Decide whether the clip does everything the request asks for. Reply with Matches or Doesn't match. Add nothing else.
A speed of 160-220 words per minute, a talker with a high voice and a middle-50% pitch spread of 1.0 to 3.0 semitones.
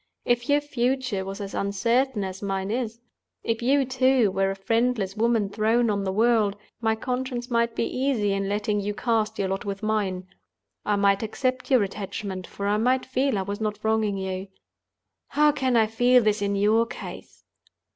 Doesn't match